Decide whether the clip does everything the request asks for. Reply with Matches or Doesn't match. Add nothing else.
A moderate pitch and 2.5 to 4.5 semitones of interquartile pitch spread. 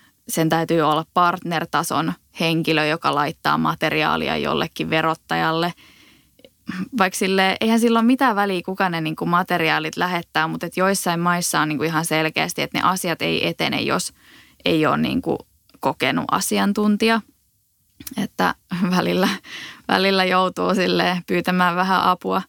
Matches